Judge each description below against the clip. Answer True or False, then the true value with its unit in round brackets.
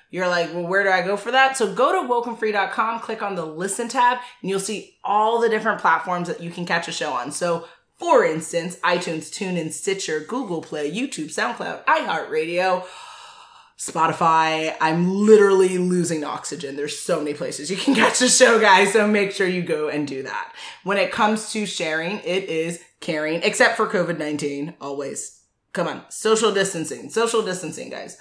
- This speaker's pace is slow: False (180 wpm)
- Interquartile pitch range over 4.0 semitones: True (5.2 semitones)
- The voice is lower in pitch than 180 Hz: False (185 Hz)